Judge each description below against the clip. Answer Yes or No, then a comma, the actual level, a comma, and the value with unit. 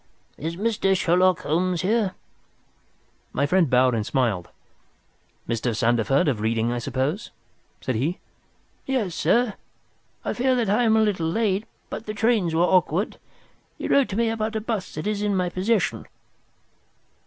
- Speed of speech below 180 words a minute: Yes, average, 155 wpm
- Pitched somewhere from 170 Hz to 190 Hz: Yes, medium, 185 Hz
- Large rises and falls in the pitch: Yes, wide, 7.5 semitones